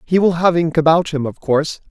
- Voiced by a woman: No, male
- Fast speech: Yes, fast, 250 wpm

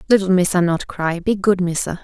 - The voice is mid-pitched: Yes, medium, 180 Hz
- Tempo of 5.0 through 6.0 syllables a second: Yes, 5.5 syllables/s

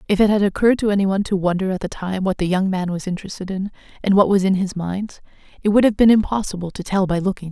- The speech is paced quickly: Yes, fast, 290 wpm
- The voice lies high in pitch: Yes, high, 195 Hz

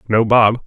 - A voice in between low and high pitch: No, low, 115 Hz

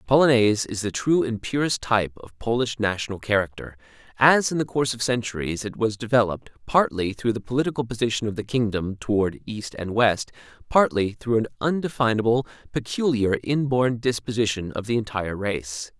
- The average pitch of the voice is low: Yes, low, 115 Hz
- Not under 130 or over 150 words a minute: No, average, 165 wpm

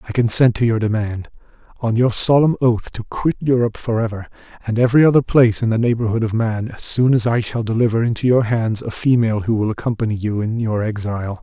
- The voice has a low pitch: Yes, low, 115 Hz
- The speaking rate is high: Yes, fast, 210 wpm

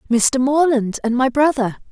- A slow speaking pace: No, average, 155 wpm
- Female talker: Yes, female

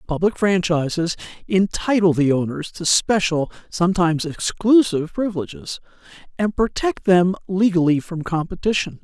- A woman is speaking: No, male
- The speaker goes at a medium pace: No, slow, 105 wpm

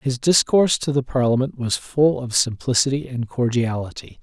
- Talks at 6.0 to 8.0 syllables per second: No, 5.0 syllables/s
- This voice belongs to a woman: No, male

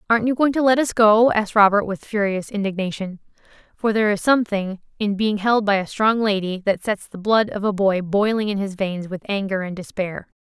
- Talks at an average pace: No, fast, 220 wpm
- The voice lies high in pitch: Yes, high, 205 Hz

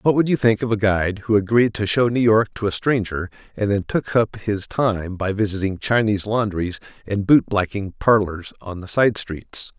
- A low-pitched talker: Yes, low, 105 Hz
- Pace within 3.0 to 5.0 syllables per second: Yes, 4.9 syllables/s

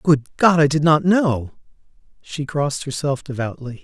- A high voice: No, medium, 145 Hz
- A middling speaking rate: Yes, average, 155 wpm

